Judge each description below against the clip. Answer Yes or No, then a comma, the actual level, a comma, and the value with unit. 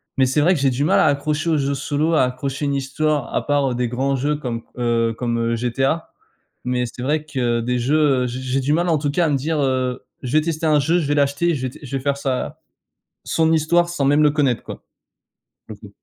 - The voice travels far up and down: No, average, 3.3 semitones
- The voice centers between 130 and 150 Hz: Yes, medium, 140 Hz